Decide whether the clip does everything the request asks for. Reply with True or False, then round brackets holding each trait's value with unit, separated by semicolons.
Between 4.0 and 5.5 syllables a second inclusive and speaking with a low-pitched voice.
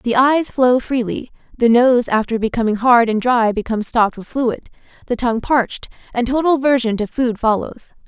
False (5.4 syllables/s; 240 Hz)